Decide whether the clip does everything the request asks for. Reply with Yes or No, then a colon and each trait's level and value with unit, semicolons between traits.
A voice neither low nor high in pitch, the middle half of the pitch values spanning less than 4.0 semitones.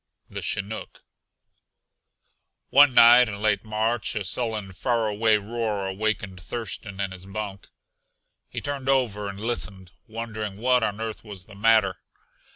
No: low, 110 Hz; narrow, 2.6 semitones